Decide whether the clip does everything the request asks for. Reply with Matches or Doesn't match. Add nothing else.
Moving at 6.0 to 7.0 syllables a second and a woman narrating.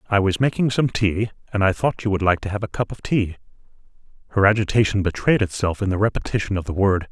Doesn't match